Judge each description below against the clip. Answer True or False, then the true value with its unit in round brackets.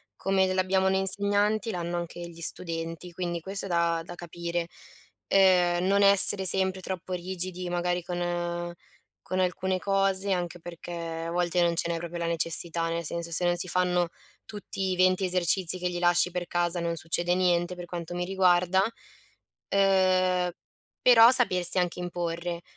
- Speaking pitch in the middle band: True (175 Hz)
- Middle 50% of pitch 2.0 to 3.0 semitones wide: False (1.5 semitones)